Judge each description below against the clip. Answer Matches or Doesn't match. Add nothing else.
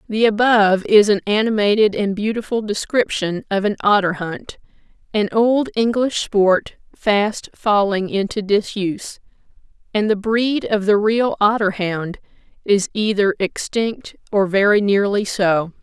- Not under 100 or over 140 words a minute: Matches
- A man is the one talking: Doesn't match